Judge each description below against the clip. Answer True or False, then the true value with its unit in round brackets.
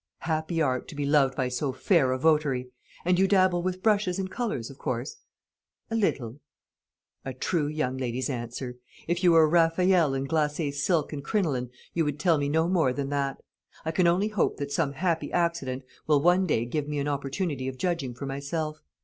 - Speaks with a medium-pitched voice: True (150 Hz)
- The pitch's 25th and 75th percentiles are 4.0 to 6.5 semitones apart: True (4.3 semitones)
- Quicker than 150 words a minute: True (200 wpm)